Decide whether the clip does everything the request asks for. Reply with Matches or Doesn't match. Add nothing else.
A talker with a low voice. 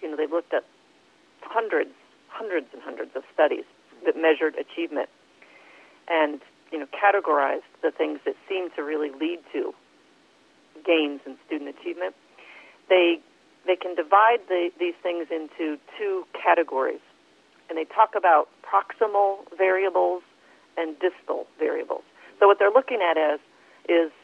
Doesn't match